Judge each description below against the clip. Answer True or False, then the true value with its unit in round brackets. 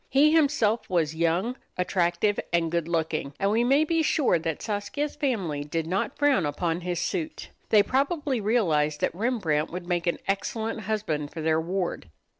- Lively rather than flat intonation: True (6.6 semitones)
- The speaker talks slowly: False (170 wpm)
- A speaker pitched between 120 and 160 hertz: False (185 Hz)